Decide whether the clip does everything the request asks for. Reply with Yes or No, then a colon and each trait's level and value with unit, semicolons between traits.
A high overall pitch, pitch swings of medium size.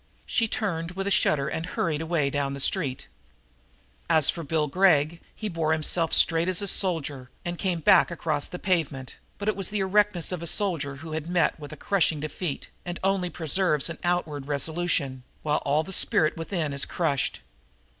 No: medium, 165 Hz; average, 3.5 semitones